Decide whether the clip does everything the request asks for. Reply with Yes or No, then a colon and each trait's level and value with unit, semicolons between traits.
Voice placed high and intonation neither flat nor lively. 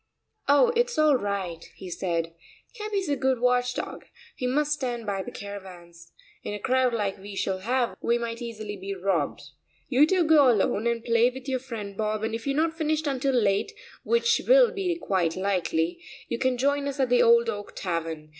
No: high, 235 Hz; wide, 5.9 semitones